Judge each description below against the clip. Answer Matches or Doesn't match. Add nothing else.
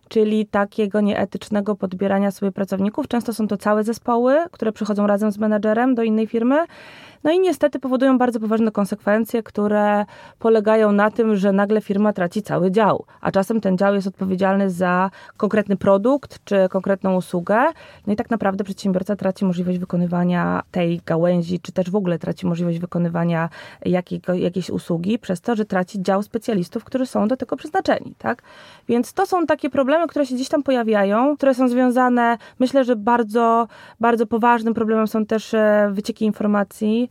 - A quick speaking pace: Matches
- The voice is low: Doesn't match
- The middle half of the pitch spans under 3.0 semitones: Doesn't match